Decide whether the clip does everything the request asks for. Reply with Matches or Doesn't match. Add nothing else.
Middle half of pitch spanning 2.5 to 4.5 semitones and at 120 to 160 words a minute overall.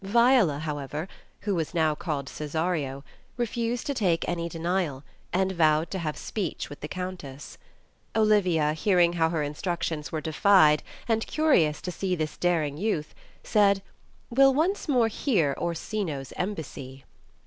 Doesn't match